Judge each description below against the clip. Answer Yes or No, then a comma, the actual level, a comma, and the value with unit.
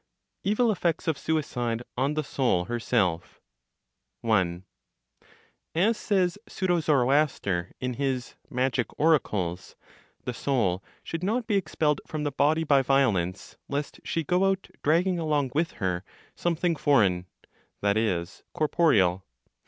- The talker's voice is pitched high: No, medium, 140 Hz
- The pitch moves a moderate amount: No, wide, 7.4 semitones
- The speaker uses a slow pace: Yes, slow, 125 wpm